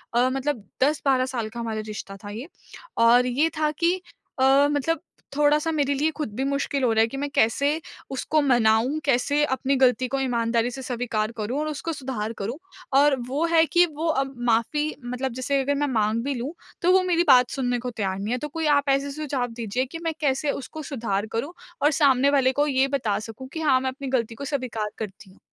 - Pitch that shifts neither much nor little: Yes, average, 3.7 semitones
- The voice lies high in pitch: Yes, very high, 265 Hz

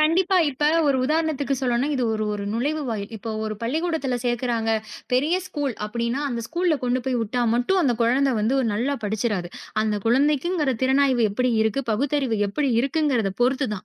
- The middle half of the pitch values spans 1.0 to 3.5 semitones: No, average, 4.0 semitones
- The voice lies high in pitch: Yes, very high, 255 Hz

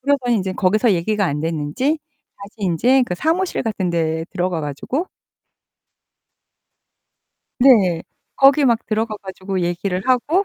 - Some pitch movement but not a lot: No, wide, 6.6 semitones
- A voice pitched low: No, high, 200 Hz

